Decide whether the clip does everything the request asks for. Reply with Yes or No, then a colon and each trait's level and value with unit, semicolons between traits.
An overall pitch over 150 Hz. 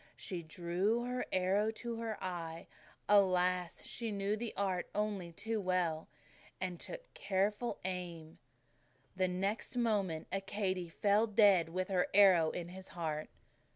Yes: high, 190 Hz